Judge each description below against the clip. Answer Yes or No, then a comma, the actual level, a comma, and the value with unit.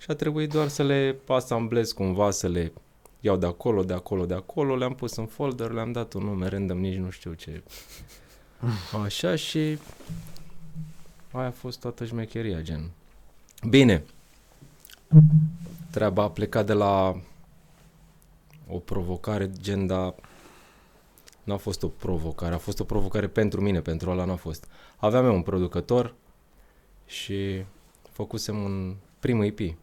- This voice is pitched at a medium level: No, low, 105 Hz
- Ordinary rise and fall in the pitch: No, wide, 6.1 semitones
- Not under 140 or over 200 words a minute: Yes, average, 145 wpm